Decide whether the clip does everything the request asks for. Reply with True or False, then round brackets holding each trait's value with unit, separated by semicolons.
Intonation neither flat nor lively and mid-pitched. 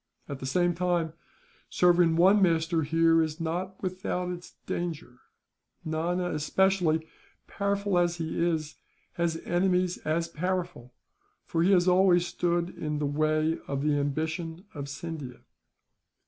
False (2.3 semitones; 170 Hz)